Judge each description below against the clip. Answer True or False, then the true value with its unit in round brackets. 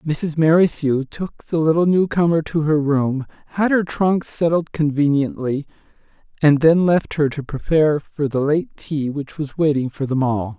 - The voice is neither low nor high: True (150 Hz)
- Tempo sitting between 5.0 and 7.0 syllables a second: False (4.4 syllables/s)